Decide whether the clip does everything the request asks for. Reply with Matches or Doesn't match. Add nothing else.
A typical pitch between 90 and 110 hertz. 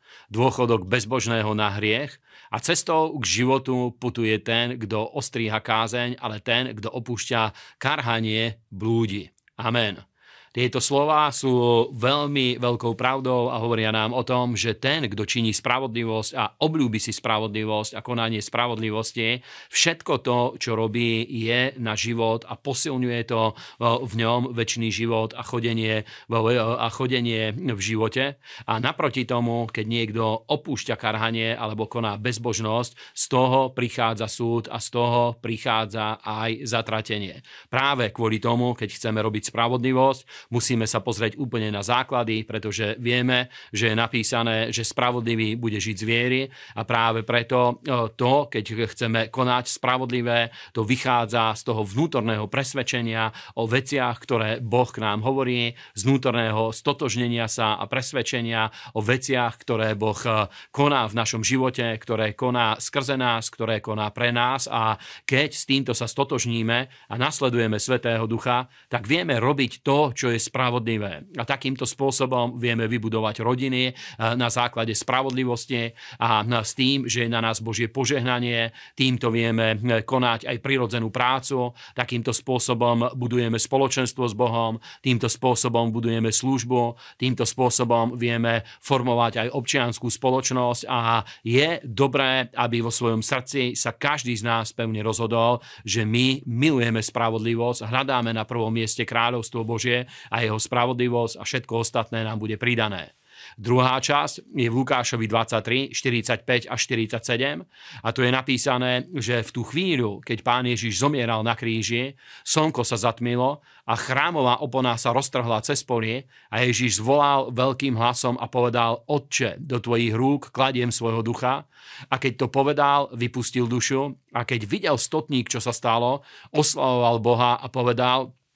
Doesn't match